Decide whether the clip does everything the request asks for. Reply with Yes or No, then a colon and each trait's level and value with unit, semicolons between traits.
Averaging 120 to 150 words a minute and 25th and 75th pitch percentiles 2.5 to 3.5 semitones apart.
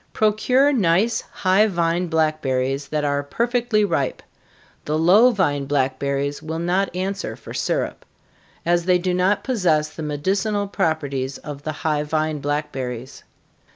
No: average, 140 wpm; average, 5.2 semitones